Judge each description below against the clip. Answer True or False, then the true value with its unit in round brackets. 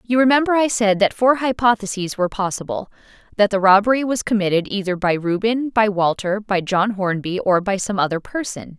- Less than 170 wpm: False (185 wpm)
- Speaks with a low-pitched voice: False (210 Hz)